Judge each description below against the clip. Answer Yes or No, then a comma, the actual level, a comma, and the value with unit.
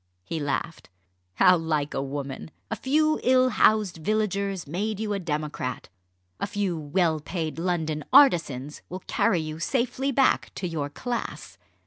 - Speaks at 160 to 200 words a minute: No, average, 145 wpm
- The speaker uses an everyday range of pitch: No, wide, 5.8 semitones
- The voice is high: No, medium, 175 Hz